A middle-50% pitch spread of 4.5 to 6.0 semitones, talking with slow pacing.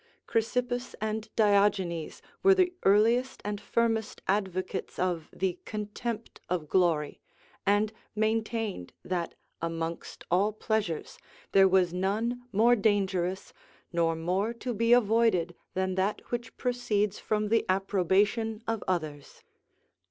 No: average, 3.6 semitones; slow, 115 wpm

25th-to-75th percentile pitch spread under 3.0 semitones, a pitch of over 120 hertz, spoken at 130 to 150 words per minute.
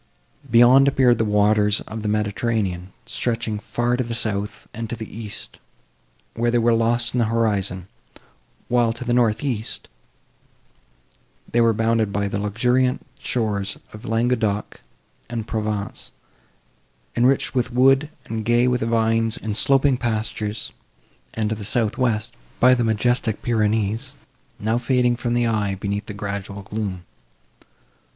No: narrow, 2.4 semitones; low, 115 Hz; average, 145 wpm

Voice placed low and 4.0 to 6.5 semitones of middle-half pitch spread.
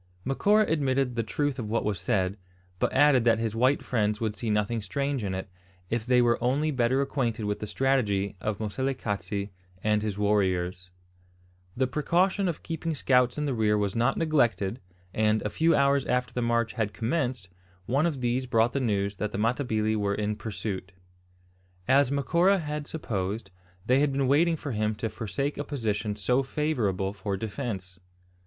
Yes: low, 115 Hz; average, 4.7 semitones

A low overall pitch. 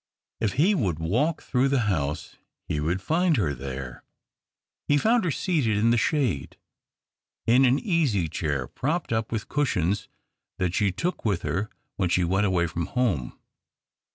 Yes: low, 105 Hz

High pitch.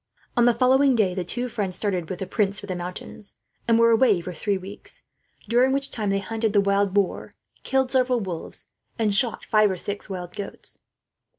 Yes: high, 205 Hz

